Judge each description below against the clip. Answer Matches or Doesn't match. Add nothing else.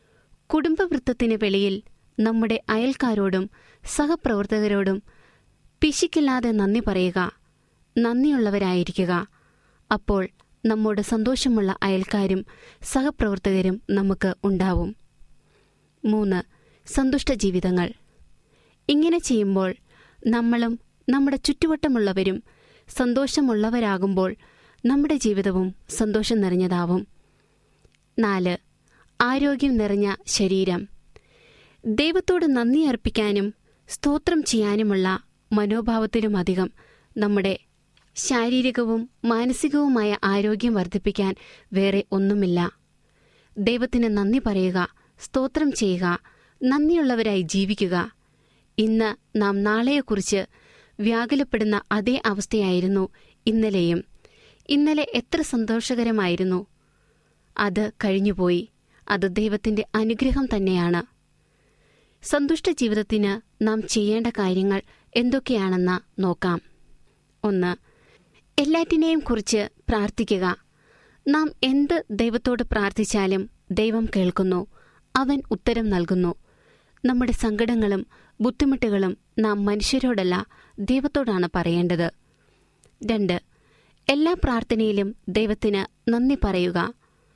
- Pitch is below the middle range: Doesn't match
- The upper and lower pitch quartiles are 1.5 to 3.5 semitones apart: Doesn't match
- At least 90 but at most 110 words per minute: Doesn't match